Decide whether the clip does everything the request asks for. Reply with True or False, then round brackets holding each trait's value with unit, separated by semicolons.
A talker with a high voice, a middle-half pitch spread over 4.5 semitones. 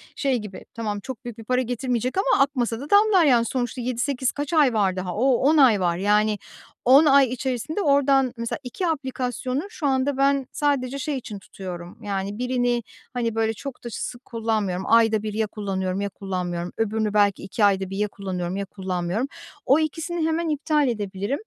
True (235 Hz; 5.1 semitones)